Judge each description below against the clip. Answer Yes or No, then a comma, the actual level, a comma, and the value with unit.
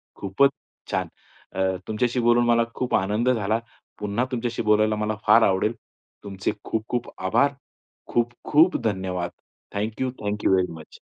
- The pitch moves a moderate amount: Yes, average, 3.5 semitones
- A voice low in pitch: Yes, low, 110 Hz